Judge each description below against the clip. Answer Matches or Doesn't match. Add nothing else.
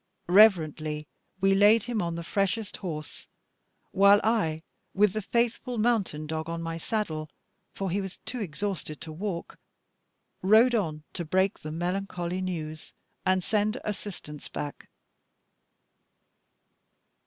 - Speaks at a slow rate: Matches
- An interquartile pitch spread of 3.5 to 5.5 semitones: Matches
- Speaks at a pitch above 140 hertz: Matches